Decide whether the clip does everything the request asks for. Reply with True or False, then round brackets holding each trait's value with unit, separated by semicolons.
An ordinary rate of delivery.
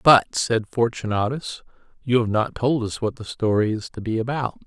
True (195 wpm)